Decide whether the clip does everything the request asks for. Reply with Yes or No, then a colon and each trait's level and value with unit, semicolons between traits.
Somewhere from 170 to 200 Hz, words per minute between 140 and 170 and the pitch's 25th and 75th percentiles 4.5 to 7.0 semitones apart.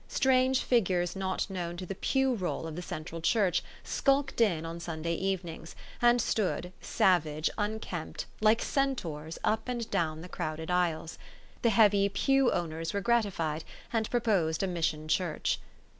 Yes: medium, 185 Hz; average, 150 wpm; average, 5.3 semitones